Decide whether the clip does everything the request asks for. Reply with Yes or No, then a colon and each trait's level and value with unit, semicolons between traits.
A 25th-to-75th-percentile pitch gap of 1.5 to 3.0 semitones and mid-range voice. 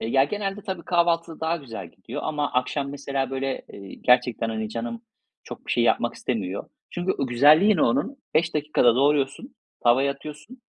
No: average, 5.0 semitones; medium, 145 Hz